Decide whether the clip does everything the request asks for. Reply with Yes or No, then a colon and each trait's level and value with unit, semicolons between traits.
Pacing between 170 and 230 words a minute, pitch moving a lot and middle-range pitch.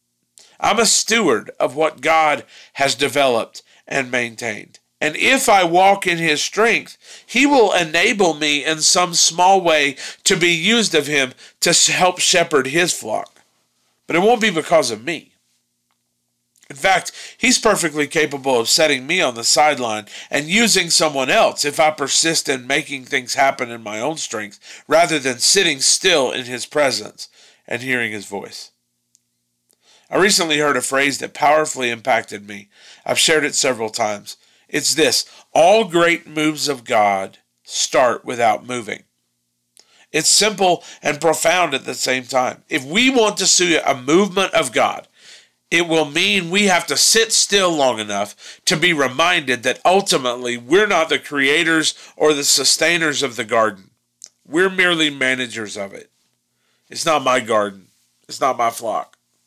No: average, 160 wpm; wide, 6.5 semitones; medium, 145 Hz